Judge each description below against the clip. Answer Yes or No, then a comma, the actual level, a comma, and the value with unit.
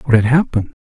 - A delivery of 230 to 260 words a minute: No, fast, 215 wpm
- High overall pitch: No, low, 125 Hz